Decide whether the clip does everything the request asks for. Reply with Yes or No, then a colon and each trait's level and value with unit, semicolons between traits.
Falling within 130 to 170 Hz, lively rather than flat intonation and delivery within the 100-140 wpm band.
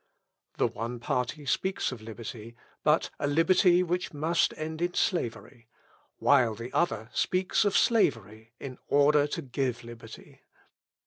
Yes: medium, 140 Hz; wide, 6.1 semitones; slow, 135 wpm